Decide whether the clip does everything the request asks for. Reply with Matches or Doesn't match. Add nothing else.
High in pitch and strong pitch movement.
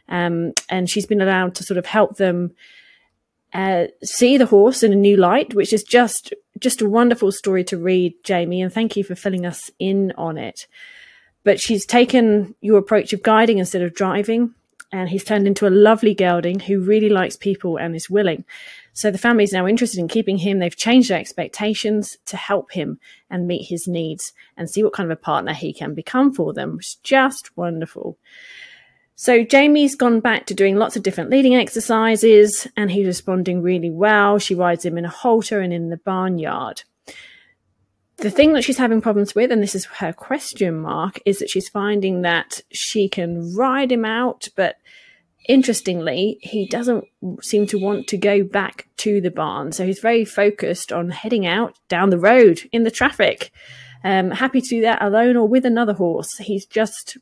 Doesn't match